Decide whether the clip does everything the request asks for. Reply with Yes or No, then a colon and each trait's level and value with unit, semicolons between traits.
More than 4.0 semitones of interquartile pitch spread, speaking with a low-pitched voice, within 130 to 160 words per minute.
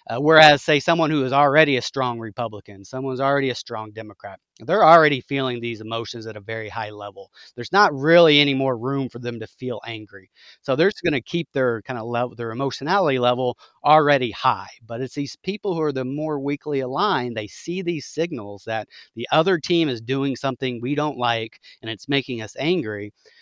No: average, 4.4 semitones; low, 130 Hz; fast, 205 wpm